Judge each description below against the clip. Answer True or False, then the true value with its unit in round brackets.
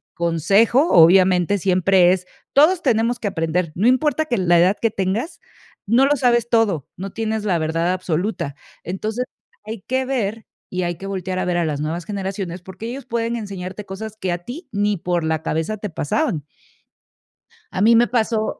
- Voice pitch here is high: True (195 Hz)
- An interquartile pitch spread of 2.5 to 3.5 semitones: False (4.6 semitones)